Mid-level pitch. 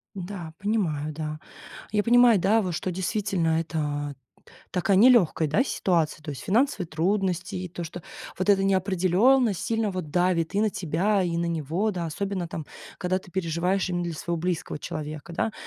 Yes: medium, 180 Hz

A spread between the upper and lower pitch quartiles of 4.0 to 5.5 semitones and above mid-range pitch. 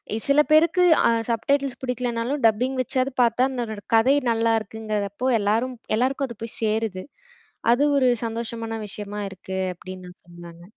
No: average, 3.5 semitones; high, 230 Hz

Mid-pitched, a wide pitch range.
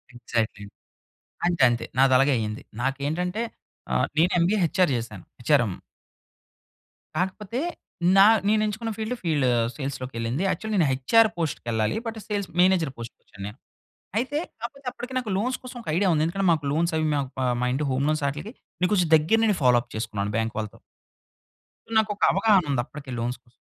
Yes: medium, 155 Hz; wide, 8.5 semitones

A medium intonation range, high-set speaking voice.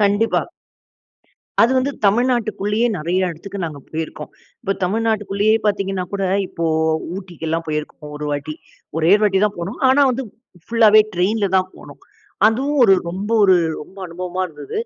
Yes: average, 4.0 semitones; high, 195 Hz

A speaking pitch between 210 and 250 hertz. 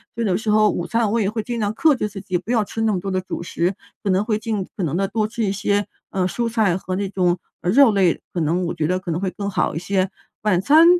No: high, 200 Hz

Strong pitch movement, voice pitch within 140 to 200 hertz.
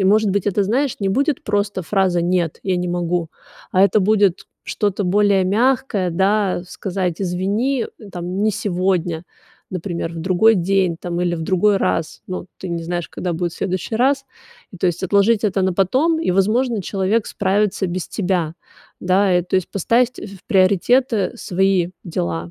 No: average, 2.8 semitones; high, 190 Hz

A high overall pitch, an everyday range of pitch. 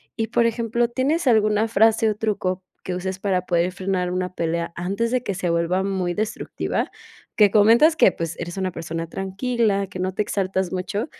Yes: high, 195 Hz; average, 3.5 semitones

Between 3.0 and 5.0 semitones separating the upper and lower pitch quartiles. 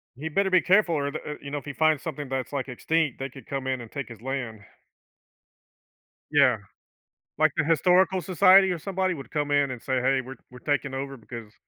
Yes: average, 3.6 semitones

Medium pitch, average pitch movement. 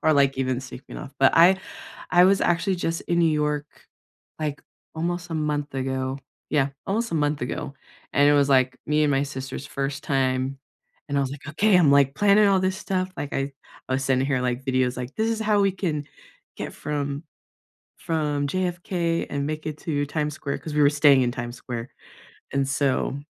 Yes: medium, 145 Hz; average, 3.7 semitones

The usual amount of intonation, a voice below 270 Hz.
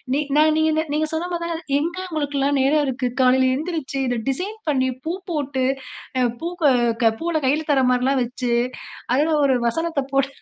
No: average, 3.3 semitones; very high, 290 Hz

